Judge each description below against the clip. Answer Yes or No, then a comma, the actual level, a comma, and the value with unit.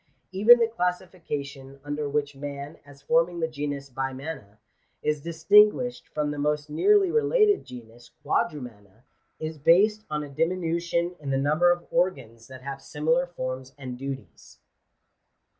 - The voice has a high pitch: No, medium, 150 Hz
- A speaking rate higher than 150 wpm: No, average, 140 wpm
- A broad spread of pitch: No, average, 4.3 semitones